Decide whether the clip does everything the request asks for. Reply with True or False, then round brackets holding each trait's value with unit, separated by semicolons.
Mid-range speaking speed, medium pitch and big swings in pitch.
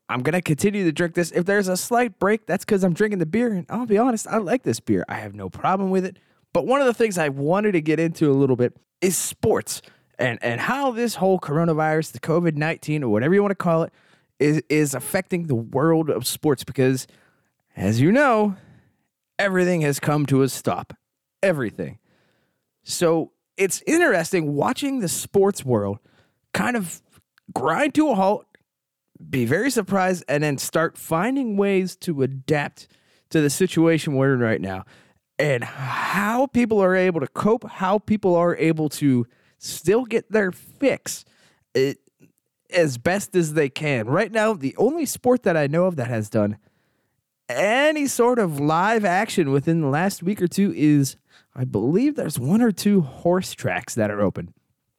True (185 wpm; 170 Hz; 6.1 semitones)